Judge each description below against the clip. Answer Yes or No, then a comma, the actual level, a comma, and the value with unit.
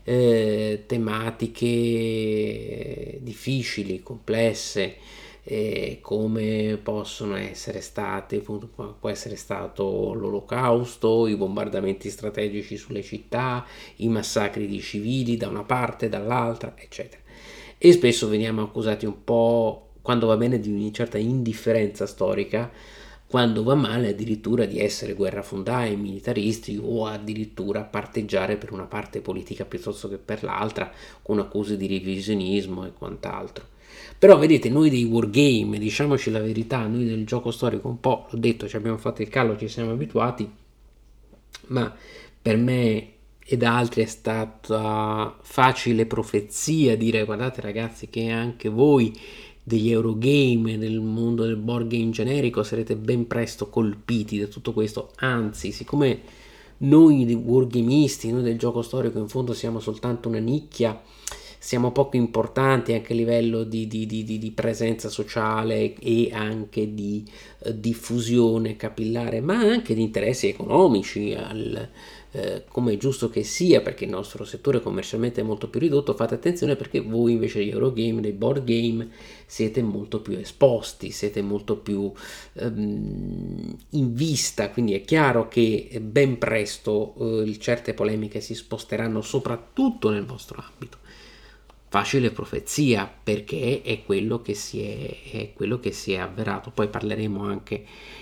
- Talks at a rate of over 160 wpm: No, average, 135 wpm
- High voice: No, low, 115 Hz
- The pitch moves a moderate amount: No, narrow, 1.9 semitones